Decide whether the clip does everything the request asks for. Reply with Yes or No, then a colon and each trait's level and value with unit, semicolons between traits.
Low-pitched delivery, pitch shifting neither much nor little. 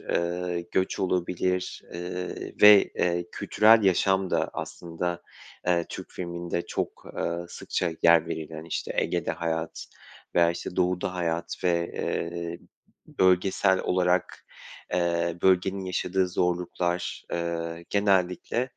No: very low, 90 Hz; narrow, 1.3 semitones